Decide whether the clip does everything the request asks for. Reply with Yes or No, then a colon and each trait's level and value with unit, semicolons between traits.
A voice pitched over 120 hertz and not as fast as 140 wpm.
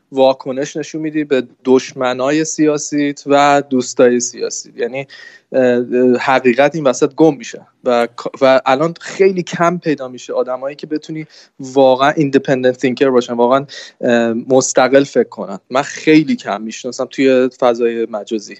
Yes: low, 135 Hz; average, 130 wpm